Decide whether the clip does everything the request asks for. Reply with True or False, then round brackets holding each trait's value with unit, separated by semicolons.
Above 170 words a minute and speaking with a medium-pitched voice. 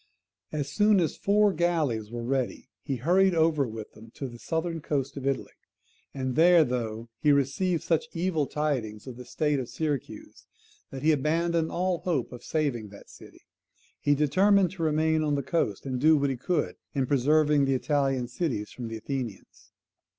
True (180 wpm; 145 Hz)